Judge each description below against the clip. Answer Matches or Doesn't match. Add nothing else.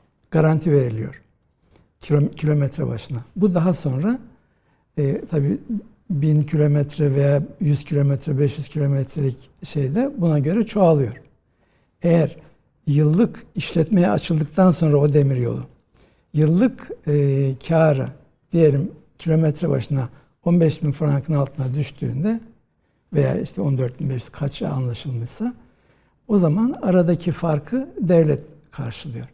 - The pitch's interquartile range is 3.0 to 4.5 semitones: Matches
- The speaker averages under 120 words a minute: Matches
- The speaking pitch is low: Doesn't match